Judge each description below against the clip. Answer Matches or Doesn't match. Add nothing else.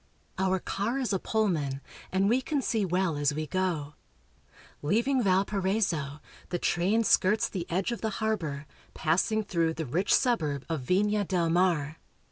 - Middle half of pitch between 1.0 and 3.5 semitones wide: Doesn't match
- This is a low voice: Doesn't match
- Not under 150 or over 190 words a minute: Matches